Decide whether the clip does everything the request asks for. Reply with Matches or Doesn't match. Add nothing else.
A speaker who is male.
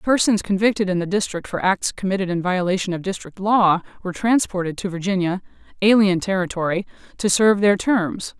Doesn't match